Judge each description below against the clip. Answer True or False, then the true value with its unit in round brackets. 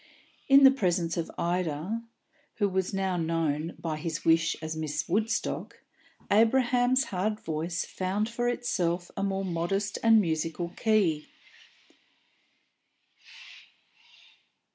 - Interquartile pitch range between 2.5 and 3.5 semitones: False (4.7 semitones)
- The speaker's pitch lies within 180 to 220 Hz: True (185 Hz)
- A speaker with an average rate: False (110 wpm)